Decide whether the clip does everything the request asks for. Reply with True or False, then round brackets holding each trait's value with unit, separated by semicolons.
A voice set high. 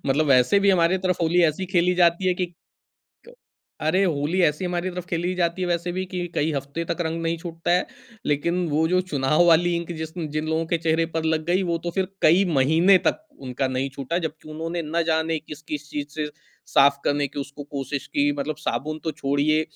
False (165 Hz)